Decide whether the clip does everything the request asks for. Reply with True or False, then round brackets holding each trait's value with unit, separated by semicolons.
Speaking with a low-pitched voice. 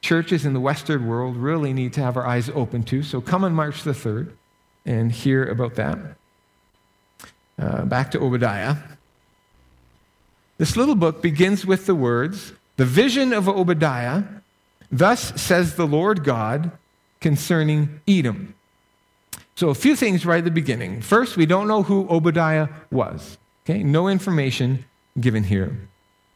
False (145 Hz)